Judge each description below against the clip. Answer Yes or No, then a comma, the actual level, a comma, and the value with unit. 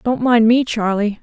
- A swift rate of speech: No, average, 195 wpm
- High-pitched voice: Yes, high, 230 Hz